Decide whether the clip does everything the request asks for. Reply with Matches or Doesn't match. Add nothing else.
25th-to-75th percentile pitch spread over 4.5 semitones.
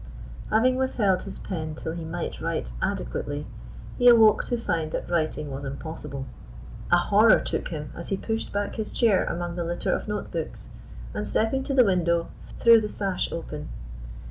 Matches